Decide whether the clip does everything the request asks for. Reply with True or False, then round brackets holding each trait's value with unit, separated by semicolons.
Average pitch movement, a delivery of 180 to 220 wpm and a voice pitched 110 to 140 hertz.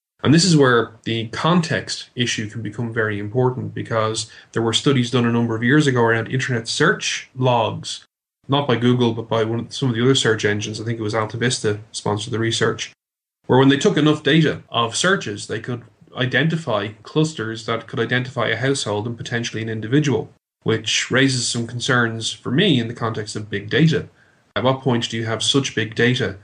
True (3.0 semitones; 200 wpm; 115 Hz)